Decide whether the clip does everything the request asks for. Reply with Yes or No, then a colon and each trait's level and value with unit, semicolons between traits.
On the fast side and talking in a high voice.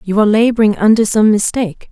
No: average, 190 wpm; high, 215 Hz